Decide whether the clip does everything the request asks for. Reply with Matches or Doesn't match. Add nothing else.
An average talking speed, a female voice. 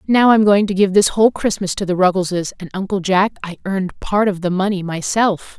Doesn't match